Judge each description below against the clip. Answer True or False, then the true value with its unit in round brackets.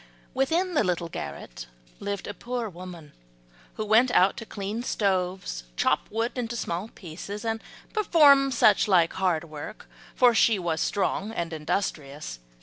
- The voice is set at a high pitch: True (200 Hz)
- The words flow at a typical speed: True (145 wpm)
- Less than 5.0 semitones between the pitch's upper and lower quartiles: False (5.3 semitones)